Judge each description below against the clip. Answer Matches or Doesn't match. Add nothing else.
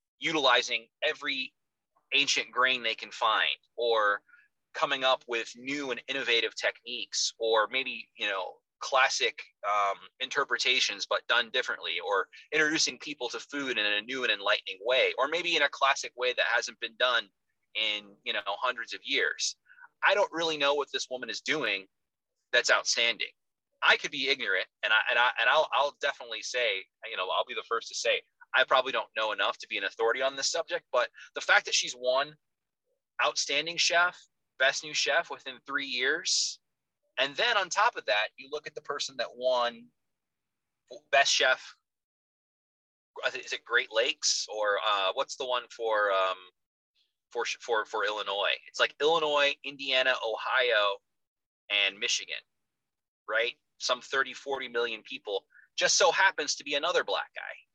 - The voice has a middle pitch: Matches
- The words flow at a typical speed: Matches